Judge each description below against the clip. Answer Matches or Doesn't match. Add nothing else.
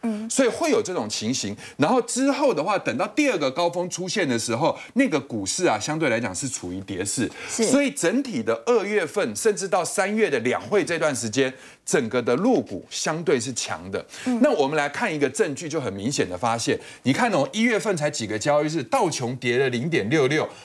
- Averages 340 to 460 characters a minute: Doesn't match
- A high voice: Matches